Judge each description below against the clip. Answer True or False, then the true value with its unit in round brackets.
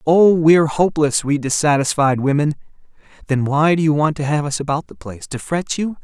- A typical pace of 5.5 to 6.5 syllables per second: True (5.6 syllables/s)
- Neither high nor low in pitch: True (150 Hz)